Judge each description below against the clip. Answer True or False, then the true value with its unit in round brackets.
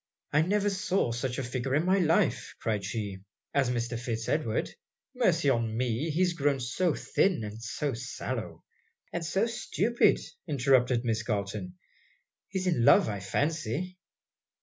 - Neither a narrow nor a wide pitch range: False (6.7 semitones)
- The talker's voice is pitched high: False (130 Hz)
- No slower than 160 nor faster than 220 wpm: False (150 wpm)